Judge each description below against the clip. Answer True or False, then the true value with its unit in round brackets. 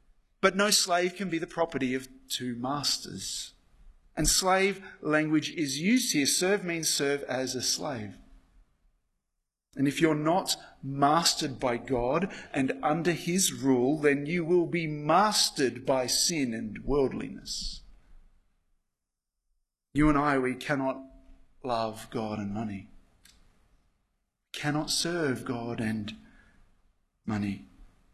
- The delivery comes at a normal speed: False (120 wpm)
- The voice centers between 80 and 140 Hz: True (135 Hz)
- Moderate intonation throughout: False (6.8 semitones)